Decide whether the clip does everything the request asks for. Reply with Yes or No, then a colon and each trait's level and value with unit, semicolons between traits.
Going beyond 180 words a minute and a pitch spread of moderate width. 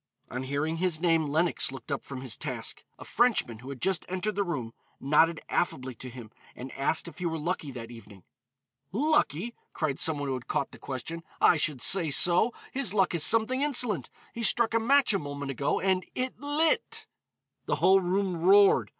No: average, 195 wpm; wide, 6.7 semitones